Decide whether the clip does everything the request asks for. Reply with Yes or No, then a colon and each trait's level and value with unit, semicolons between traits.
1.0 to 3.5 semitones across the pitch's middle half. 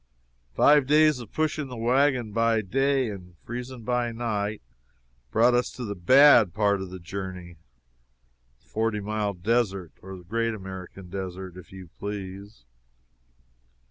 No: average, 4.3 semitones